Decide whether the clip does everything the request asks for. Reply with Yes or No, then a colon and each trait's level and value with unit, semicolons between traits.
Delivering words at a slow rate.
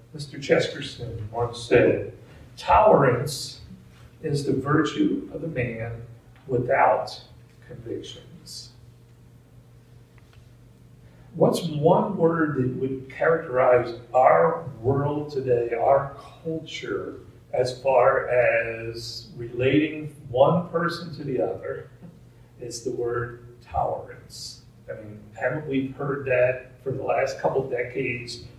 Yes: slow, 105 wpm